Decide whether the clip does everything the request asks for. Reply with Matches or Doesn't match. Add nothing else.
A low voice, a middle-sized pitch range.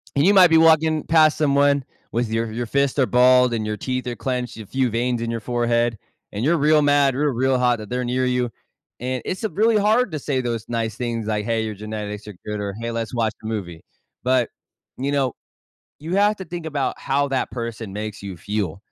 Matches